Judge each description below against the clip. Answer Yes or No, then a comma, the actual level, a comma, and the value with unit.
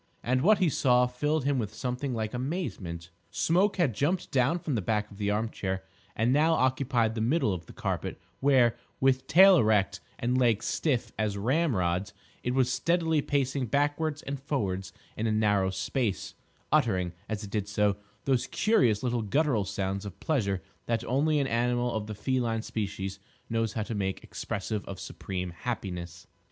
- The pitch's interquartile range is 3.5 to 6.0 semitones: Yes, average, 5.2 semitones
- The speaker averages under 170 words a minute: No, average, 175 wpm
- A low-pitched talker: Yes, low, 120 Hz